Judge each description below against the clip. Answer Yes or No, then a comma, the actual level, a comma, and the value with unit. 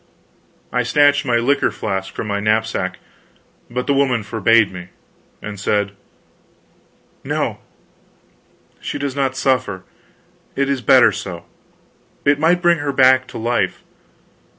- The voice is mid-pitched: No, low, 125 Hz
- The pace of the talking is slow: Yes, slow, 130 wpm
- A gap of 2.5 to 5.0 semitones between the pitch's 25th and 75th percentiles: Yes, average, 4.7 semitones